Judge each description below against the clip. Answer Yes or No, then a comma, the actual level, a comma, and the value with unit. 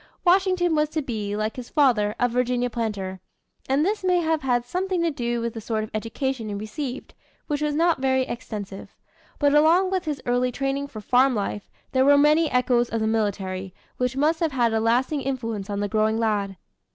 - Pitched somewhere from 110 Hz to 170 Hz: No, very high, 250 Hz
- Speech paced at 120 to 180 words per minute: No, average, 200 wpm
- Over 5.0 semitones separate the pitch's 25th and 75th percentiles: Yes, wide, 5.4 semitones